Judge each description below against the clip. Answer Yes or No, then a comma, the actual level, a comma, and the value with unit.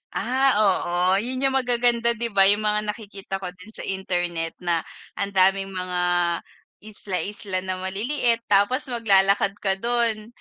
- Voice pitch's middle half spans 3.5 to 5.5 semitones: Yes, average, 3.8 semitones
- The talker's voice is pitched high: Yes, high, 200 Hz